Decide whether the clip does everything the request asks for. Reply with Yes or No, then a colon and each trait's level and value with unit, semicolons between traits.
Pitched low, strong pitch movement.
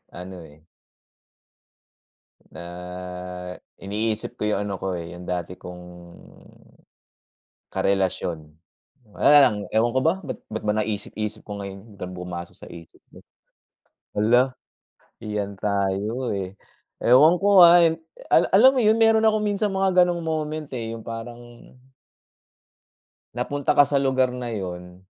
Yes: low, 110 Hz; wide, 7.9 semitones